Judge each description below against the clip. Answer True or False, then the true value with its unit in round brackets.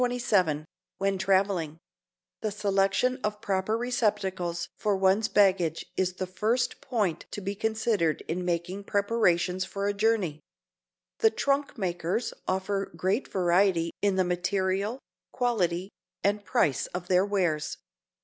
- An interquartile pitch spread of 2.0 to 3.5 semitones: True (2.8 semitones)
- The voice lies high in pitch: True (195 Hz)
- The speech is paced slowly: True (130 wpm)